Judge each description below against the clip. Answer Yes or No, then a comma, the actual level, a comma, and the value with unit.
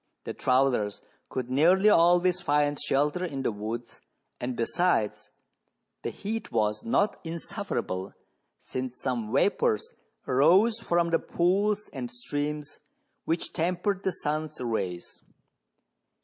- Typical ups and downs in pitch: No, wide, 6.8 semitones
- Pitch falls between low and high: Yes, medium, 150 Hz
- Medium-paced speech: No, slow, 115 wpm